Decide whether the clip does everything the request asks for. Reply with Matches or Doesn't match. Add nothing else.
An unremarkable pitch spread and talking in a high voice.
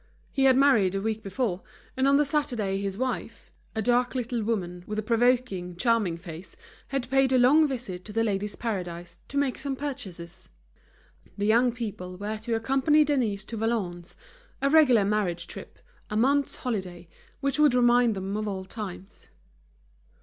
Matches